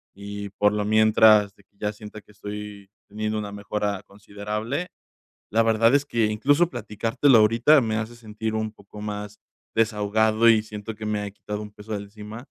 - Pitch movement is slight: Yes, narrow, 1.2 semitones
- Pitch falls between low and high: No, low, 105 Hz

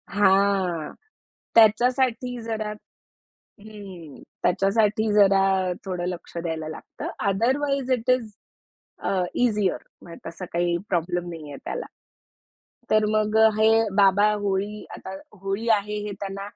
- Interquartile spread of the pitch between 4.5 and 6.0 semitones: No, average, 2.8 semitones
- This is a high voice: Yes, high, 200 Hz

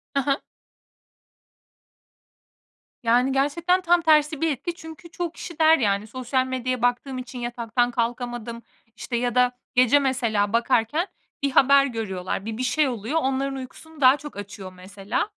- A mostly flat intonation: No, average, 3.7 semitones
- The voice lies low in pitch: No, very high, 255 Hz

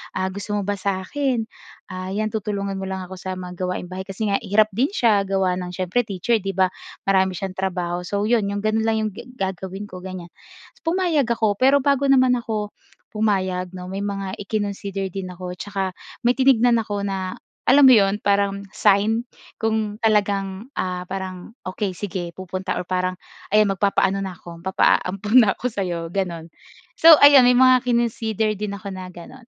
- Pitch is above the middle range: Yes, high, 200 Hz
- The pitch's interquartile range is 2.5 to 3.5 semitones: Yes, average, 2.8 semitones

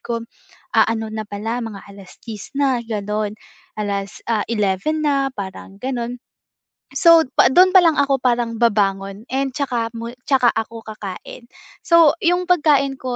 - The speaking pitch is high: Yes, high, 235 Hz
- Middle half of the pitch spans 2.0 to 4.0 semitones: No, average, 4.6 semitones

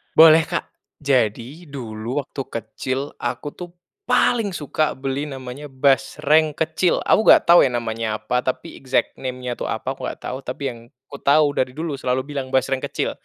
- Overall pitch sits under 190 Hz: Yes, low, 135 Hz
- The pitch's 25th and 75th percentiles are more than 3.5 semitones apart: No, average, 3.1 semitones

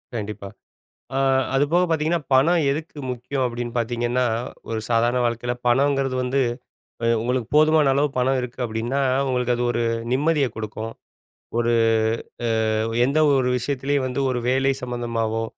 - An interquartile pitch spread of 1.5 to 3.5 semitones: Yes, average, 2.8 semitones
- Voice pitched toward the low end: Yes, low, 125 Hz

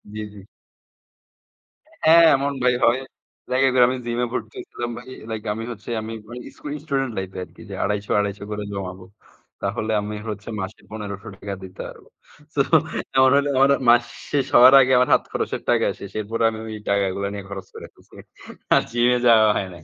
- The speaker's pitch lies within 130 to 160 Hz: No, low, 110 Hz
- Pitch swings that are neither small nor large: Yes, average, 3.9 semitones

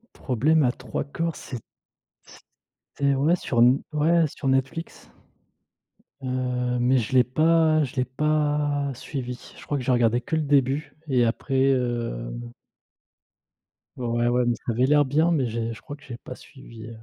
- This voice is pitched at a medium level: No, low, 130 Hz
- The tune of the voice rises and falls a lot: No, average, 3.2 semitones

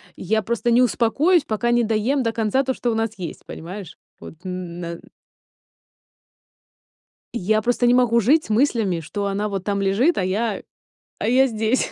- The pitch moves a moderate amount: Yes, average, 3.6 semitones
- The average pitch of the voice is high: Yes, high, 220 Hz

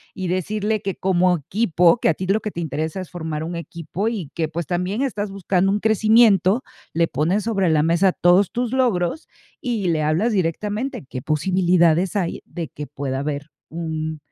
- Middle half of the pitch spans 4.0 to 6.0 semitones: Yes, average, 4.3 semitones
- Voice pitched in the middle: Yes, medium, 180 Hz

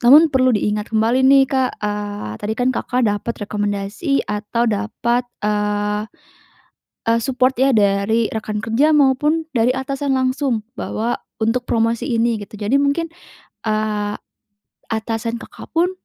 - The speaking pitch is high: Yes, high, 230 Hz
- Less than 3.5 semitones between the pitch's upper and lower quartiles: No, average, 3.8 semitones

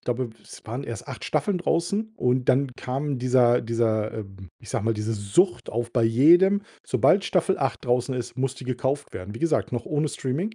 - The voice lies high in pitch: No, low, 125 Hz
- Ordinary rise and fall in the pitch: Yes, average, 4.7 semitones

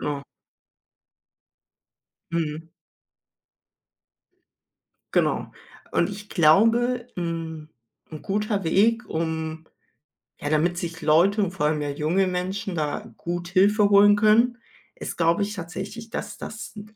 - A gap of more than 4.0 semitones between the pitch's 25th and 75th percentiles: Yes, average, 4.4 semitones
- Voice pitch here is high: No, medium, 180 Hz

